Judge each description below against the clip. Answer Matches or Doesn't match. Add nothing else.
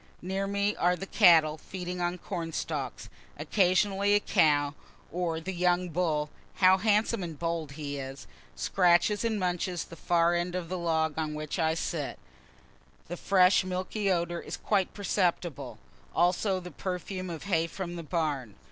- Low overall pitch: Doesn't match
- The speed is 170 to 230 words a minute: Doesn't match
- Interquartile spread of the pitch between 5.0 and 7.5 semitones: Doesn't match